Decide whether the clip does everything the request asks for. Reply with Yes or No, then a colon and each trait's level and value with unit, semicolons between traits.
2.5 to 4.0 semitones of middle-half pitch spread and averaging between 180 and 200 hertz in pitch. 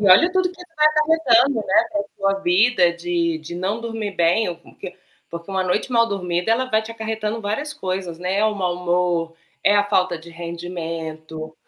No: average, 4.7 semitones; high, 190 Hz